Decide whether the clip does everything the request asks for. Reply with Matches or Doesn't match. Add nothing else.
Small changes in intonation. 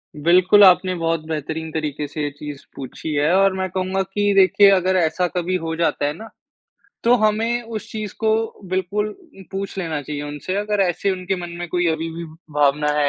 Doesn't match